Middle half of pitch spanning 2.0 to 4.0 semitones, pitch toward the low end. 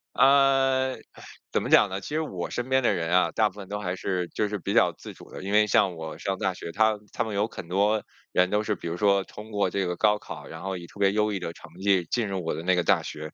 Yes: average, 2.9 semitones; low, 100 Hz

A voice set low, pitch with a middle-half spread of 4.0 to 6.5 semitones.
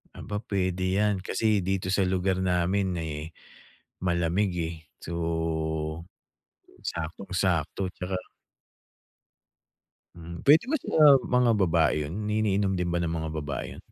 No: very low, 90 Hz; average, 3.0 semitones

